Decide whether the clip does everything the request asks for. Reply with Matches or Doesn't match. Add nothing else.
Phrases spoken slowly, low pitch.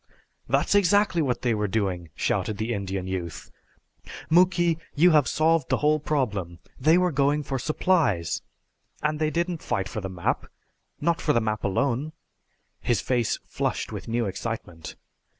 Doesn't match